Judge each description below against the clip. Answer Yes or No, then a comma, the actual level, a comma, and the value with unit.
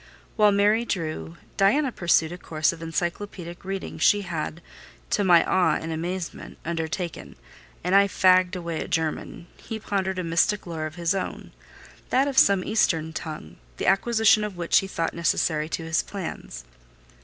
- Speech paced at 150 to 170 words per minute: Yes, average, 165 wpm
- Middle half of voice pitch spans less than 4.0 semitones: Yes, average, 3.4 semitones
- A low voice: No, medium, 175 Hz